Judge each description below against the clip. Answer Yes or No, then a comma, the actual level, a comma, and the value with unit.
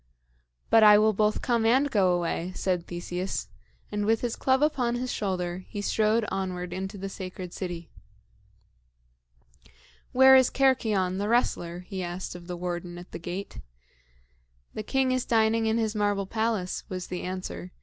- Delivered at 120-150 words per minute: No, average, 160 wpm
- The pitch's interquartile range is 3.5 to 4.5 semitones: Yes, average, 3.9 semitones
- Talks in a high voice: Yes, high, 195 Hz